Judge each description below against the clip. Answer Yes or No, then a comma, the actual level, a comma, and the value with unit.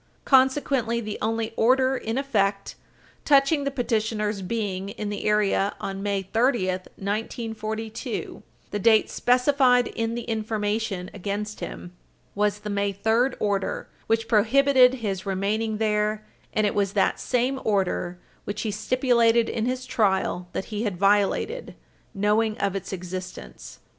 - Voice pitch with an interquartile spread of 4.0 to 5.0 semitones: No, average, 2.8 semitones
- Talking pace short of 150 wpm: Yes, average, 140 wpm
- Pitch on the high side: Yes, high, 215 Hz